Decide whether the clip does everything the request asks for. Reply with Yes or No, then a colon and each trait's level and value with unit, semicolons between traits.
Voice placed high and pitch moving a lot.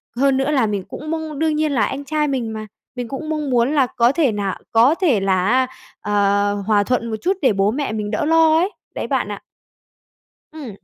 Yes: very high, 260 Hz; wide, 6.1 semitones